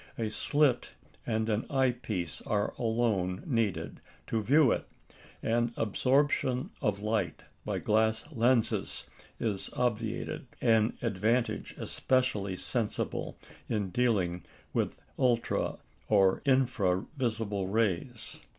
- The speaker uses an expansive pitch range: No, average, 3.2 semitones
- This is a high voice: No, low, 115 Hz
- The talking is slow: Yes, slow, 110 wpm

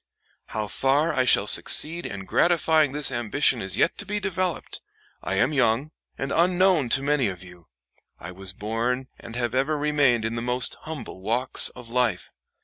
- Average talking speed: Yes, average, 175 wpm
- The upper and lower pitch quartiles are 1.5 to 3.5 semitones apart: No, average, 5.1 semitones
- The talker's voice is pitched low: Yes, low, 130 Hz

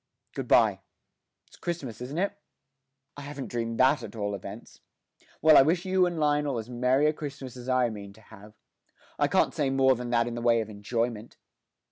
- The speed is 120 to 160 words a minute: No, average, 195 wpm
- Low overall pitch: Yes, low, 125 Hz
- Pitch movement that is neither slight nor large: Yes, average, 4.2 semitones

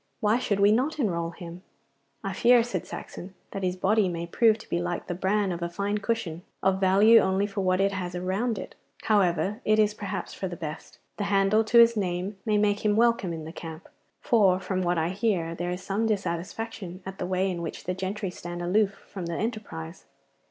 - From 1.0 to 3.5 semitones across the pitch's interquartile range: Yes, average, 3.1 semitones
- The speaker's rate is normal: No, fast, 215 wpm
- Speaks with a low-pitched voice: No, high, 190 Hz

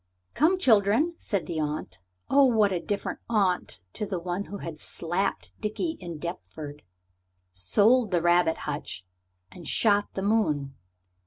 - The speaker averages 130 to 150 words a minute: Yes, average, 145 wpm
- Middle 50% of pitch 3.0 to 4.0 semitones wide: No, average, 5.1 semitones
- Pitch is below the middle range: No, medium, 185 Hz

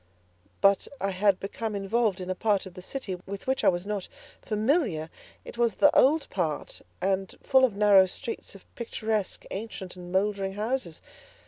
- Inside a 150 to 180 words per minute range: Yes, average, 175 wpm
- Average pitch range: Yes, average, 3.1 semitones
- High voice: Yes, high, 200 Hz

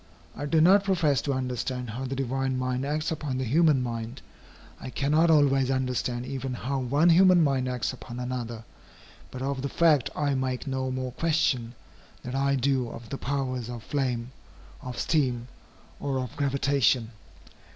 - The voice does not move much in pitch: Yes, narrow, 2.1 semitones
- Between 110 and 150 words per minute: No, average, 165 wpm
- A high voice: No, low, 130 Hz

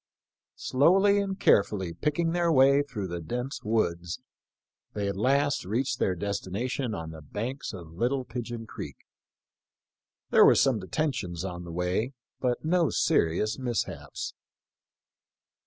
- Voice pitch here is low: Yes, low, 115 Hz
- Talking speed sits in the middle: No, slow, 130 wpm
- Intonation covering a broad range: Yes, wide, 6.8 semitones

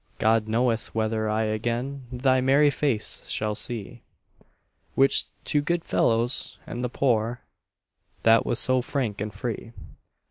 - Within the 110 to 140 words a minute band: Yes, slow, 135 wpm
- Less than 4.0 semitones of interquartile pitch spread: Yes, average, 2.9 semitones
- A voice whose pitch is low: Yes, low, 120 Hz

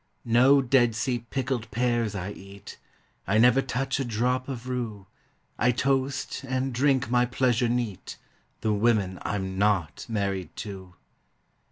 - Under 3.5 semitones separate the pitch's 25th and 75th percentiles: No, average, 3.9 semitones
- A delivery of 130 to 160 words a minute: Yes, average, 140 wpm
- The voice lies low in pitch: Yes, low, 120 Hz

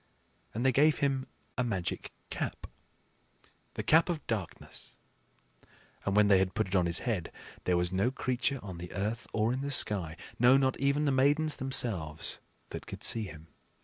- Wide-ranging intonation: Yes, wide, 6.2 semitones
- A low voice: Yes, low, 115 Hz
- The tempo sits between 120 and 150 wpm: No, average, 180 wpm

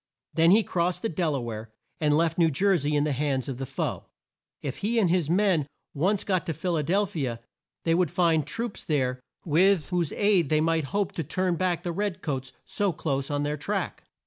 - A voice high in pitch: No, medium, 165 Hz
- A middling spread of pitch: Yes, average, 4.1 semitones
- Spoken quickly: Yes, fast, 225 wpm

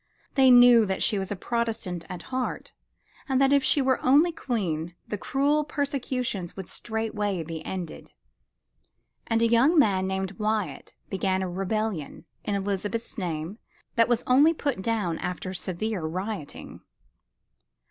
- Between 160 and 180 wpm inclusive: No, average, 140 wpm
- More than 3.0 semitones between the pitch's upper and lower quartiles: Yes, average, 5.1 semitones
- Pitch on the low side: No, high, 215 Hz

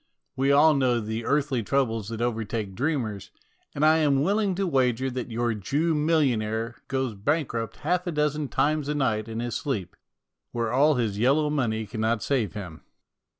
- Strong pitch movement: No, average, 4.8 semitones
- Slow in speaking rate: No, average, 175 wpm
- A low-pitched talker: Yes, low, 125 Hz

